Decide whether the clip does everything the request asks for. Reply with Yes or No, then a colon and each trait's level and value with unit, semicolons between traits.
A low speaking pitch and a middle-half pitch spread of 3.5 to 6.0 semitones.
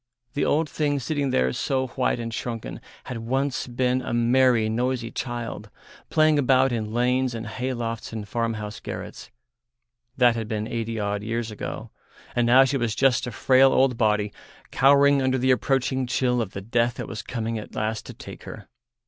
No: low, 120 Hz; narrow, 2.6 semitones